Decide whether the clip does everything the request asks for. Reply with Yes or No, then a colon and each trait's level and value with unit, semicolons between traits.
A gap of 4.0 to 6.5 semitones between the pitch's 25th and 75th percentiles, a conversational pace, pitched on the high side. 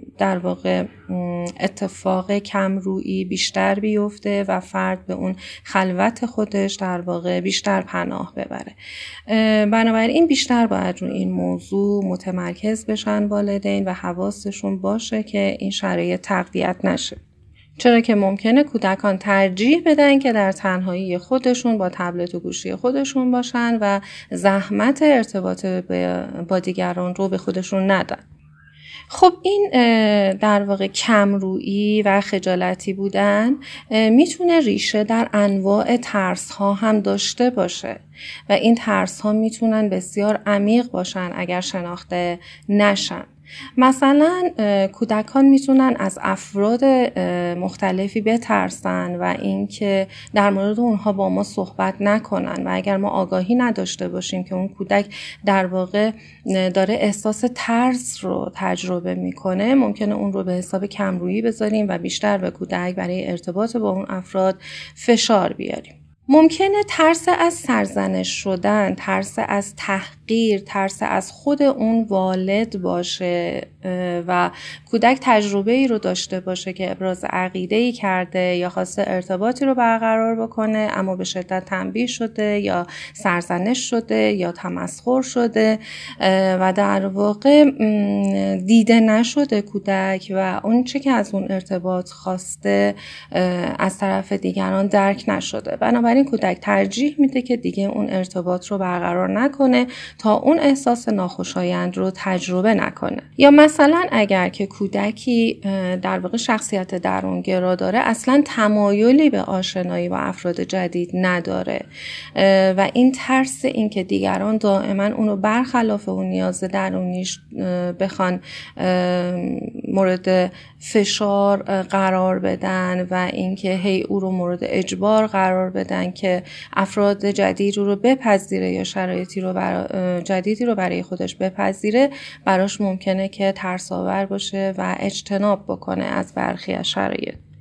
No: average, 3.2 semitones; average, 125 wpm; high, 195 Hz